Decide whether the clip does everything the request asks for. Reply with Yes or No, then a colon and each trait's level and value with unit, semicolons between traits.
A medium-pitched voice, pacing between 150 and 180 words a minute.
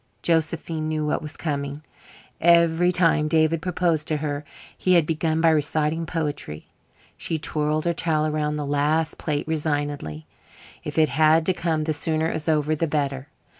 Yes: medium, 155 Hz; average, 170 wpm